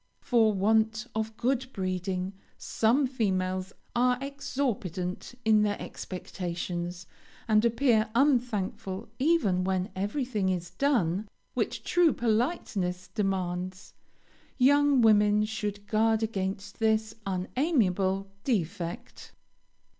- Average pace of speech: No, slow, 95 wpm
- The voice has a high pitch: Yes, high, 210 Hz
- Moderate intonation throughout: Yes, average, 4.4 semitones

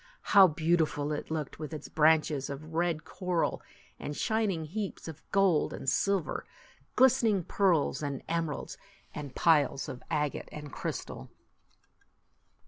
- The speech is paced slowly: Yes, slow, 130 wpm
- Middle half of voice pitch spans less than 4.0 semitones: Yes, average, 3.5 semitones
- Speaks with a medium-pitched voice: Yes, medium, 160 Hz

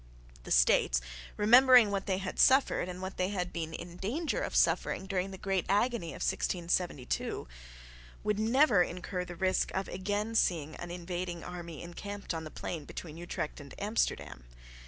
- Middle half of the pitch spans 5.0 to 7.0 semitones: No, average, 3.0 semitones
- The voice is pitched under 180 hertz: No, medium, 185 Hz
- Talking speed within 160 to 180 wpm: Yes, average, 165 wpm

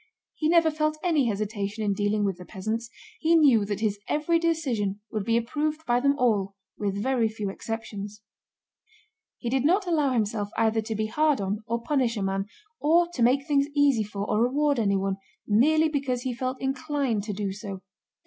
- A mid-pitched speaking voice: No, high, 235 Hz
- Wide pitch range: Yes, wide, 5.7 semitones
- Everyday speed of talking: Yes, average, 185 wpm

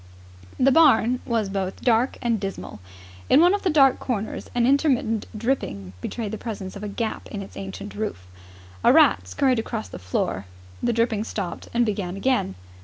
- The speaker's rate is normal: Yes, average, 180 wpm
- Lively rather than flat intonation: No, average, 4.2 semitones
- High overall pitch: Yes, high, 220 Hz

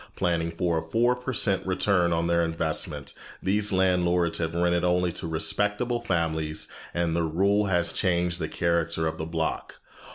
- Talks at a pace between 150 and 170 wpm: Yes, average, 165 wpm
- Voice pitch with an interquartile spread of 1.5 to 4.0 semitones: Yes, narrow, 2.4 semitones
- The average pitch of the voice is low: Yes, very low, 85 Hz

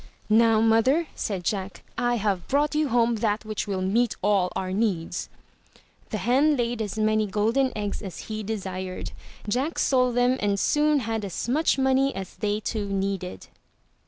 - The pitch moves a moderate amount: Yes, average, 3.7 semitones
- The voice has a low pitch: No, high, 220 Hz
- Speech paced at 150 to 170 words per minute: Yes, average, 165 wpm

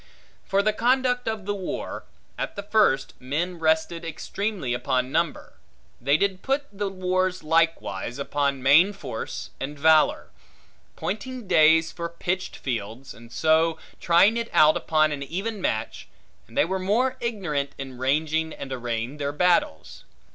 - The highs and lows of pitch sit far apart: Yes, wide, 5.8 semitones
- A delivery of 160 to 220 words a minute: No, average, 145 wpm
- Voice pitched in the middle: Yes, medium, 165 Hz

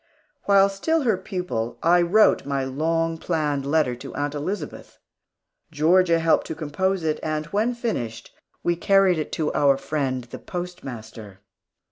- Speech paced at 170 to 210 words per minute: No, average, 145 wpm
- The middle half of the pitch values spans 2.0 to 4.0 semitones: No, average, 4.8 semitones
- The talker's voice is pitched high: No, medium, 160 Hz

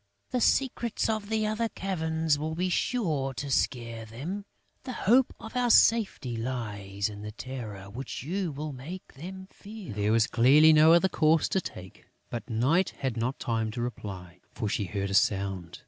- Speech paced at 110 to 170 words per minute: No, average, 180 wpm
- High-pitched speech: No, low, 135 Hz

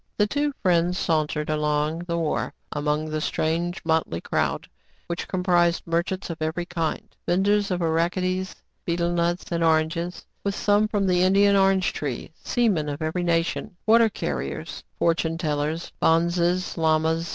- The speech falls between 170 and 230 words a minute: No, average, 150 wpm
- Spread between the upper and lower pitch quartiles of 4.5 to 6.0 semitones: No, narrow, 2.5 semitones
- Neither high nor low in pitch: Yes, medium, 170 Hz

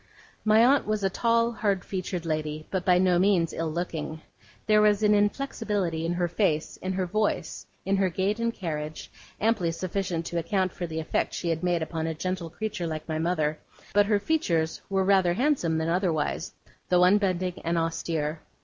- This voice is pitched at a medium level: Yes, medium, 180 Hz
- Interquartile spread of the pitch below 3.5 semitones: No, average, 3.8 semitones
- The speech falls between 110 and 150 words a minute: No, average, 185 wpm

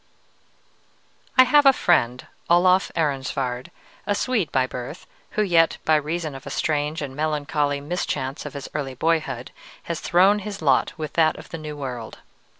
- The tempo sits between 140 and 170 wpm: Yes, average, 160 wpm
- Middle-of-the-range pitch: Yes, medium, 150 Hz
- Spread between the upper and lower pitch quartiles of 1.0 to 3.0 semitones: No, average, 4.1 semitones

